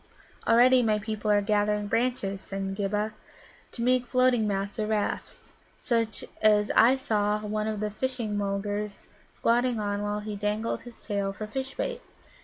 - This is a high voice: Yes, high, 210 Hz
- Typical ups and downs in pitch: No, narrow, 2.2 semitones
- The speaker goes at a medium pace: Yes, average, 160 wpm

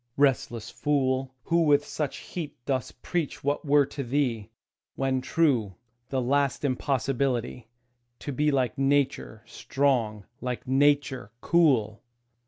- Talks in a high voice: No, low, 135 Hz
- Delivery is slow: Yes, slow, 120 wpm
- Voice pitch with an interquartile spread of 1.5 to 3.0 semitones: Yes, narrow, 2.5 semitones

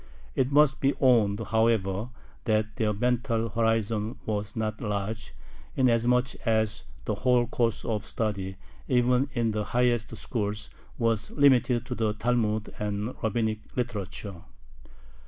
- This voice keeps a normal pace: No, slow, 125 wpm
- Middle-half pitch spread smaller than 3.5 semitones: Yes, narrow, 2.6 semitones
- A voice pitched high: No, low, 115 Hz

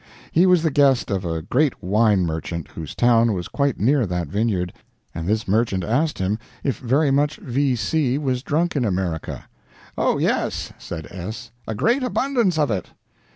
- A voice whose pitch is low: Yes, low, 115 Hz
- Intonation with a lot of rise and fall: Yes, wide, 7.5 semitones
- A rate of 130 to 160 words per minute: No, average, 175 wpm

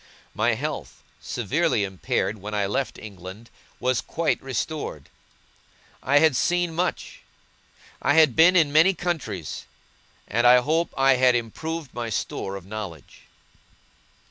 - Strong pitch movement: Yes, wide, 7.3 semitones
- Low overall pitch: Yes, low, 125 Hz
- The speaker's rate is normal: No, slow, 130 wpm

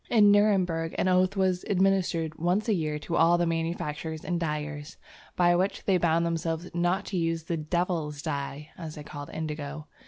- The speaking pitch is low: No, medium, 165 Hz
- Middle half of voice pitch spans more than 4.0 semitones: No, average, 2.8 semitones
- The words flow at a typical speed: Yes, average, 180 wpm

